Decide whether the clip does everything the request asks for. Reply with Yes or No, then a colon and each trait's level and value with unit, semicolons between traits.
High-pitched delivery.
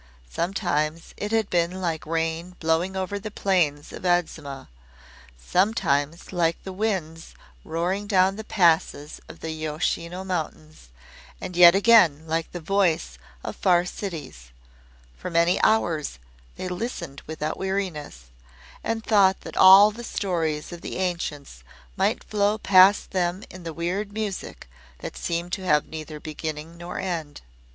No: medium, 175 Hz